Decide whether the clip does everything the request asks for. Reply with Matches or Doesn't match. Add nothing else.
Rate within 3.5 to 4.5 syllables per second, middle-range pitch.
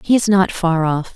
Doesn't match